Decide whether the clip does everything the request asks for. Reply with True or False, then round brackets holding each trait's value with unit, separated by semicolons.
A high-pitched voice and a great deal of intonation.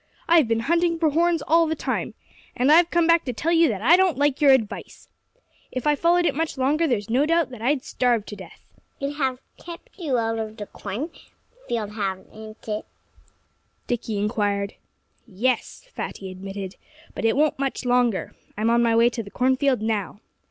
True (255 Hz; 6.5 semitones)